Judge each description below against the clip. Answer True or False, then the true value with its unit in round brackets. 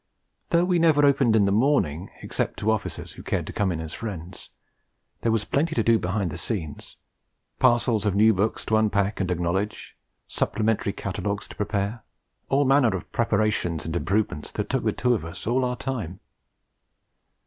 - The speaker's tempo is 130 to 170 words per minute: False (180 wpm)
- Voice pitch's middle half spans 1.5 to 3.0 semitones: False (3.9 semitones)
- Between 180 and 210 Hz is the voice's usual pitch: False (105 Hz)